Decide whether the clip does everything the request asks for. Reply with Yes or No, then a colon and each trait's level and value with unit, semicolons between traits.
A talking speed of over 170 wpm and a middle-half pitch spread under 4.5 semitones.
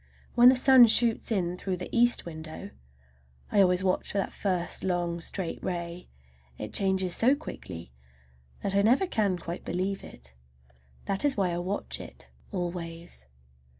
No: average, 150 wpm; average, 3.4 semitones